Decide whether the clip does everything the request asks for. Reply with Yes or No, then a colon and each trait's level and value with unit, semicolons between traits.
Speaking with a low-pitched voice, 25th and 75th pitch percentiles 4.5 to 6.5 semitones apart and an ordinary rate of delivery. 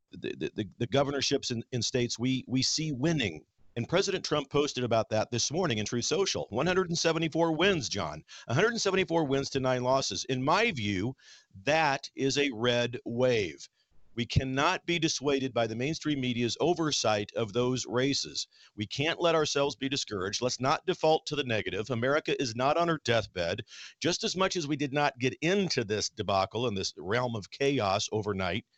Yes: low, 130 Hz; average, 4.9 semitones; average, 175 wpm